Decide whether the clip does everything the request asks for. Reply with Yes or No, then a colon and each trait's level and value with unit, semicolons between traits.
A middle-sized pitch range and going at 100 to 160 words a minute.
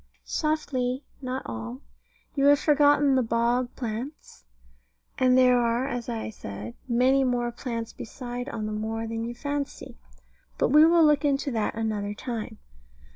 Yes: average, 3.4 semitones; average, 150 wpm